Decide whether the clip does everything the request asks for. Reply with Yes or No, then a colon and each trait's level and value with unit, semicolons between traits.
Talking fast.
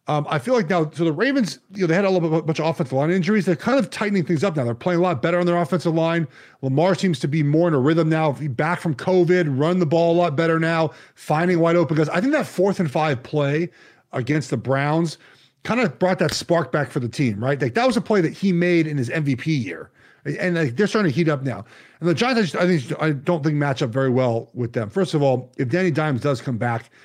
Yes: fast, 270 wpm